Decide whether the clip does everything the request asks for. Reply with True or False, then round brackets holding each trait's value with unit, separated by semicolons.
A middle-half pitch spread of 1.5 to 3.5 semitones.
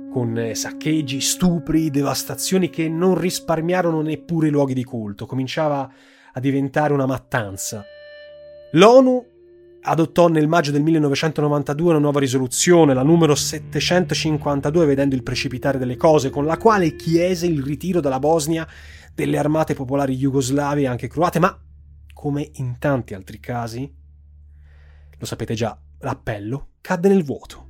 False (4.3 semitones)